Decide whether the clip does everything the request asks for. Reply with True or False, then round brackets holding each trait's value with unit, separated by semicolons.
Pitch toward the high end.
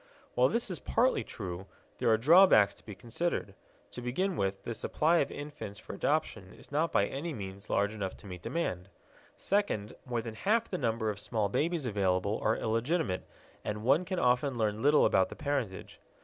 False (115 Hz)